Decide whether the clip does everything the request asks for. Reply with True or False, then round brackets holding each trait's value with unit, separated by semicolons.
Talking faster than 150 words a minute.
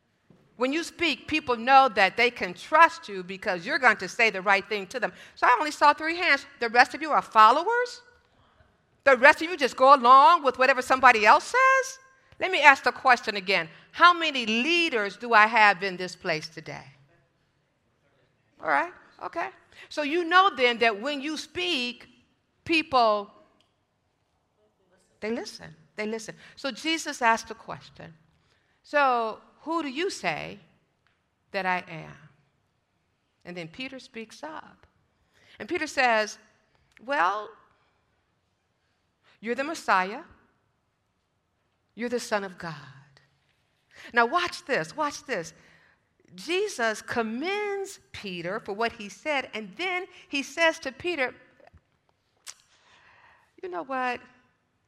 False (140 wpm)